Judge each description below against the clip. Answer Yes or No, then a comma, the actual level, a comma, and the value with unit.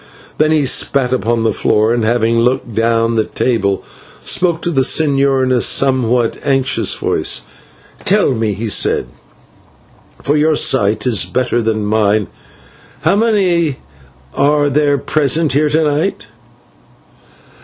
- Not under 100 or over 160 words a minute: Yes, slow, 135 wpm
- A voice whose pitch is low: Yes, low, 130 Hz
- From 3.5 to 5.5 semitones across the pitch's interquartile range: Yes, average, 4.7 semitones